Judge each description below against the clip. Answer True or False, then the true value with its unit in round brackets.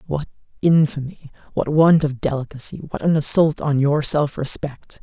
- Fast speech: False (155 wpm)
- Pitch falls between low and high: True (145 Hz)